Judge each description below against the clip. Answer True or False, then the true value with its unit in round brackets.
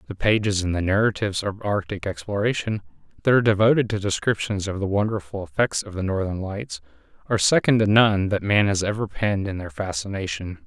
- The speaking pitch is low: True (100 Hz)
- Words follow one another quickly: False (185 wpm)